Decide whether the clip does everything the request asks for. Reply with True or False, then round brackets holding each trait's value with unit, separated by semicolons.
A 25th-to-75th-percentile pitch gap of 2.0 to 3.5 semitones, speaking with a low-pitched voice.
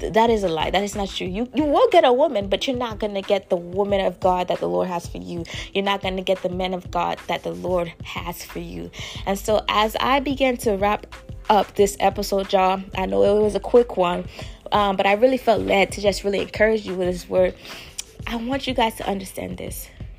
False (3.1 semitones; 195 Hz)